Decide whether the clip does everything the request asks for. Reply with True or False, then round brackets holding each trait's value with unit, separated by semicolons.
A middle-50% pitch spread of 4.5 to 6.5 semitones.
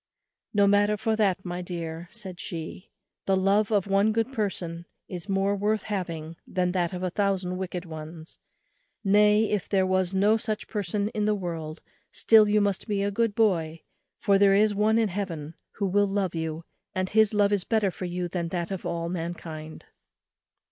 False (3.0 semitones)